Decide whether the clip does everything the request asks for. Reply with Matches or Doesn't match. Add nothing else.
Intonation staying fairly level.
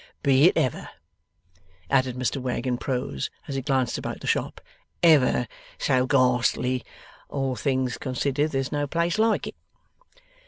Matches